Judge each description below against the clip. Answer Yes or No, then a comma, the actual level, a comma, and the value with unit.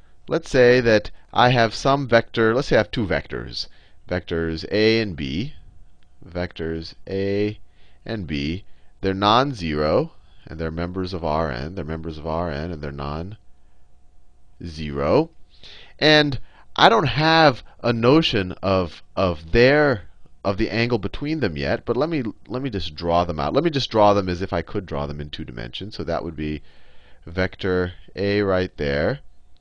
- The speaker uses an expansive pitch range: Yes, wide, 6.0 semitones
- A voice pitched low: Yes, very low, 90 Hz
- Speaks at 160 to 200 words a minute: Yes, average, 170 wpm